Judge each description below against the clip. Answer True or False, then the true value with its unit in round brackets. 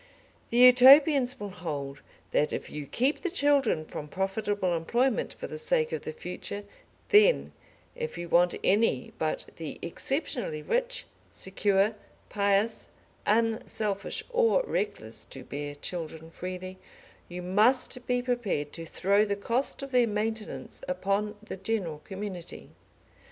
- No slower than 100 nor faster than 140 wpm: True (135 wpm)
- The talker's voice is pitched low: False (205 Hz)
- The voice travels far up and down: True (6.0 semitones)